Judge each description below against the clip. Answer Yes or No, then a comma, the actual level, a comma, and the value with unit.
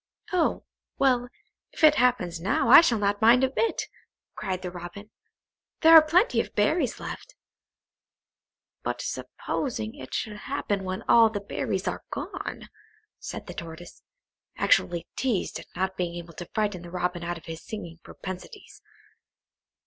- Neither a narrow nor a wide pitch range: No, wide, 6.1 semitones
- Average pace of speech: Yes, average, 150 wpm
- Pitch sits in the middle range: No, high, 205 Hz